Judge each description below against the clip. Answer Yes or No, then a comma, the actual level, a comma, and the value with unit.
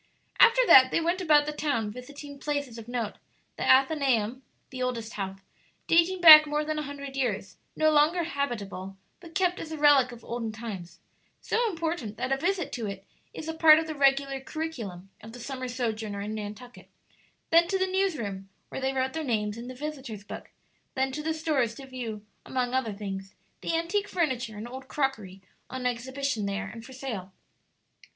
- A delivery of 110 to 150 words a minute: No, average, 190 wpm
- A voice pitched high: Yes, very high, 260 Hz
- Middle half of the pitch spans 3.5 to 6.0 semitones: Yes, wide, 5.6 semitones